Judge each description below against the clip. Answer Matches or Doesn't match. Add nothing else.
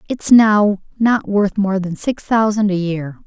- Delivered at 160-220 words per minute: Matches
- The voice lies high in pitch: Matches